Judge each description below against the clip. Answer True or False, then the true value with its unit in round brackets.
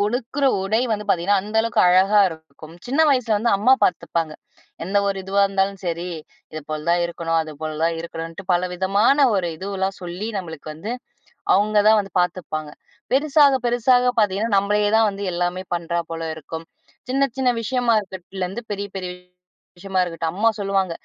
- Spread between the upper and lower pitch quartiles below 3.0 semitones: False (4.0 semitones)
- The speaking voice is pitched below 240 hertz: True (195 Hz)